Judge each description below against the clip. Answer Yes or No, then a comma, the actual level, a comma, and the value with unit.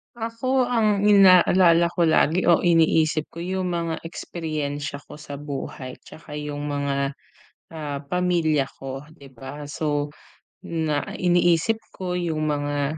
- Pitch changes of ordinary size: Yes, average, 3.5 semitones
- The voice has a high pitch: No, medium, 160 Hz